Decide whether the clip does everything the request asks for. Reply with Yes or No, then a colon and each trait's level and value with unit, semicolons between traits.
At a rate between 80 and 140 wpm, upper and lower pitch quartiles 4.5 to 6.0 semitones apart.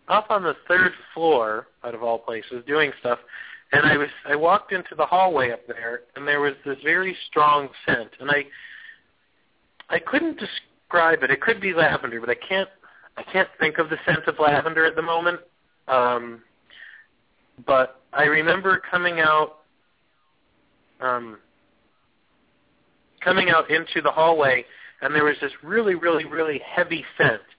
No: average, 155 wpm; average, 4.8 semitones